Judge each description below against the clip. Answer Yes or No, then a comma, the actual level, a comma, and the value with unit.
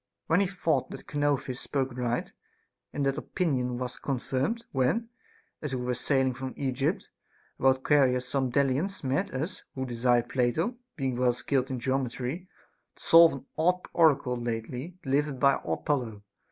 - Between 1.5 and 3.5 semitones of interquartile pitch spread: Yes, average, 2.8 semitones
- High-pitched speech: No, low, 135 Hz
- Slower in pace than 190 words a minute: Yes, average, 155 wpm